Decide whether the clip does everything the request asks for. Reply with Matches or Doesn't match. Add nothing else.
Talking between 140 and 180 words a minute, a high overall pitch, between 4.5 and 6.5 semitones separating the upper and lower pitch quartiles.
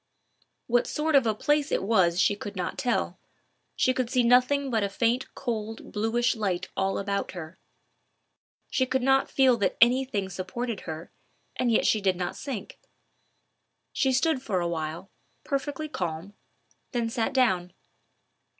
Matches